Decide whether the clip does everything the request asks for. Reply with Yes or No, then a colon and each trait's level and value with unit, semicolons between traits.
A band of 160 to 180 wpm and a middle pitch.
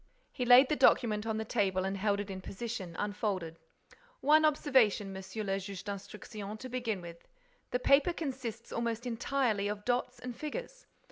No: average, 165 wpm; high, 220 Hz